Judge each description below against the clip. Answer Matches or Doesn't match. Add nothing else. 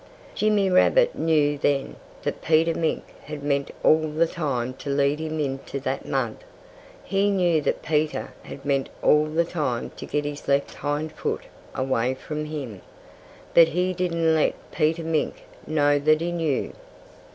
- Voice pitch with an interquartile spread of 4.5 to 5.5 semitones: Doesn't match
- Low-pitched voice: Doesn't match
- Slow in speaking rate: Doesn't match